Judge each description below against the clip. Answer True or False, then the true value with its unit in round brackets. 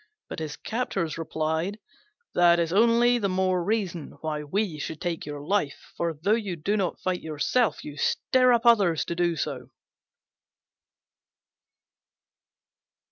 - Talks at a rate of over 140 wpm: False (135 wpm)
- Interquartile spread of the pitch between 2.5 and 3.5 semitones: False (4.6 semitones)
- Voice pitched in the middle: True (175 Hz)